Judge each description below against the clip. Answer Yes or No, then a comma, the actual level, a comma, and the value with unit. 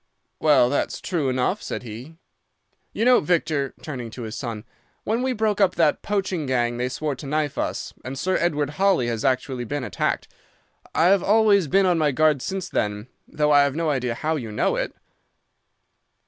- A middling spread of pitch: No, wide, 6.1 semitones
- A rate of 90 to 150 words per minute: No, average, 185 wpm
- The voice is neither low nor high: Yes, medium, 150 Hz